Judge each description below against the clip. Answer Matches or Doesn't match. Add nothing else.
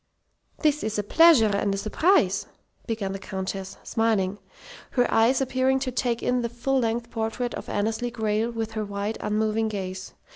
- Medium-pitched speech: Doesn't match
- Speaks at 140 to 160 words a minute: Doesn't match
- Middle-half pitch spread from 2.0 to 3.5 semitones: Matches